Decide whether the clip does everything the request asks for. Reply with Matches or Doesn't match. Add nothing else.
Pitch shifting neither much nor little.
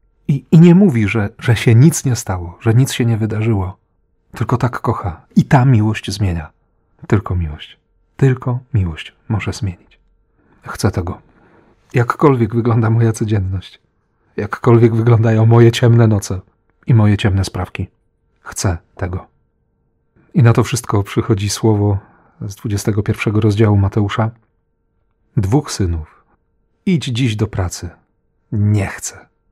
Matches